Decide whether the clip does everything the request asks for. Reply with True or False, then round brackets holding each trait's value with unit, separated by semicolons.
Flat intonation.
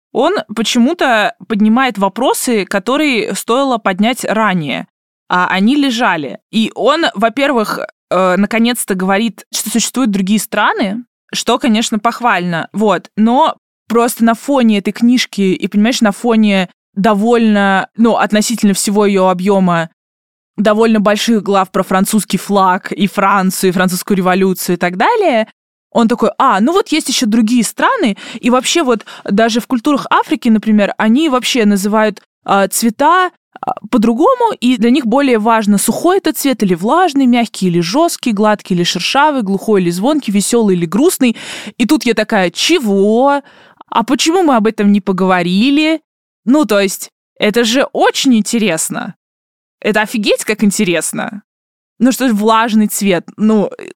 False (3.9 semitones)